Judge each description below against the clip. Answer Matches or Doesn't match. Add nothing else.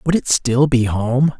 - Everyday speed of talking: Doesn't match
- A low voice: Matches